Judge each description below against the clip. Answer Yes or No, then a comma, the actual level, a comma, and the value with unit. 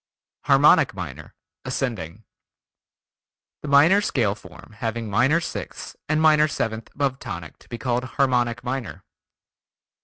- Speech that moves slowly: Yes, slow, 120 wpm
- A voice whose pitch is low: Yes, low, 125 Hz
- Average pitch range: Yes, average, 4.1 semitones